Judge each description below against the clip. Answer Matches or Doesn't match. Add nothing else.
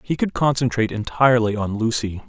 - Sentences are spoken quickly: Doesn't match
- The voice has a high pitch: Doesn't match